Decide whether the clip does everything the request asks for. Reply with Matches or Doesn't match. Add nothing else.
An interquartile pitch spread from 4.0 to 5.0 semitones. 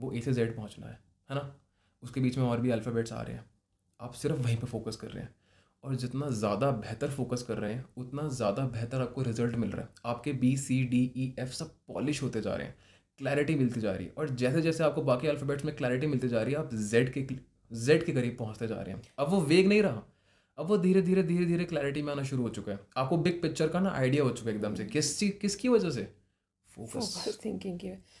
Matches